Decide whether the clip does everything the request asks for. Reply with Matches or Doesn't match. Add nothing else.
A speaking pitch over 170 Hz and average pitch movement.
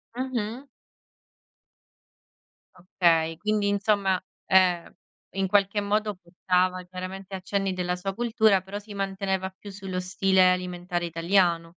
Doesn't match